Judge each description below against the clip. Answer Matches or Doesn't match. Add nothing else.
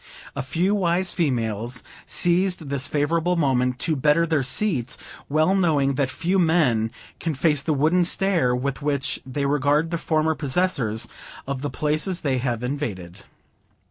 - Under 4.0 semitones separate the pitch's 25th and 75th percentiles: Doesn't match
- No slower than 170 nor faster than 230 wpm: Doesn't match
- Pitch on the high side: Doesn't match